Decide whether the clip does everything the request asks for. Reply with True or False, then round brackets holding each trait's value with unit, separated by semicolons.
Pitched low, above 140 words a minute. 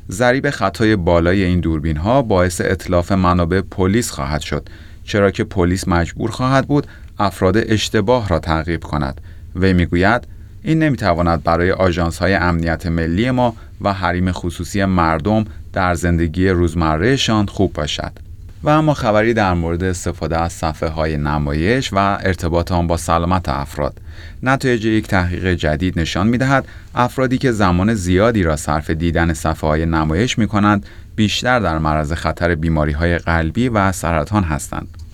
True (90 Hz; 150 wpm)